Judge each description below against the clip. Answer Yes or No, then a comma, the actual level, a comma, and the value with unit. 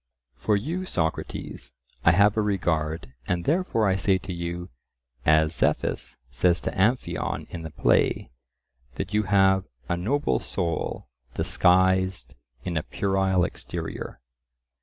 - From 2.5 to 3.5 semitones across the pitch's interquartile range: Yes, average, 2.9 semitones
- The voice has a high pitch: No, very low, 95 Hz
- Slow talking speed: Yes, slow, 130 wpm